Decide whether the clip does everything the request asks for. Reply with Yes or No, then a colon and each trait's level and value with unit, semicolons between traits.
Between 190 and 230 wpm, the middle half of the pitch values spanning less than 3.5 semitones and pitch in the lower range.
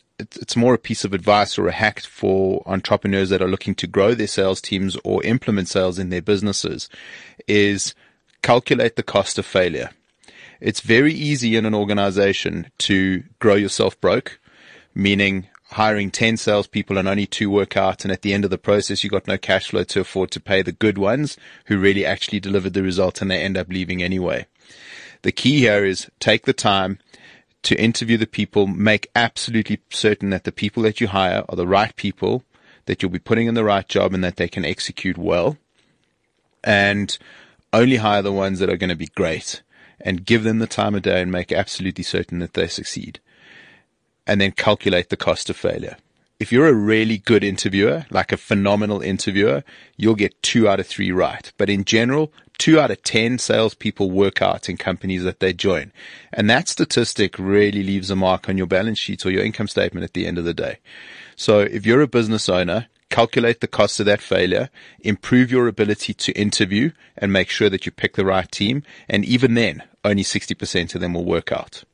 Yes: average, 200 wpm; narrow, 2.5 semitones; low, 100 Hz